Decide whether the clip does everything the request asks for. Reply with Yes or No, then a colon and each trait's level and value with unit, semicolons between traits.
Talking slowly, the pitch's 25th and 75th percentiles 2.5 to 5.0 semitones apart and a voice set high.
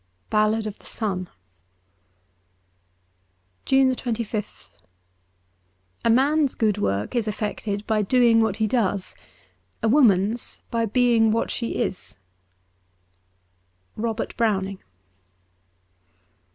Yes: slow, 100 wpm; average, 3.3 semitones; high, 215 Hz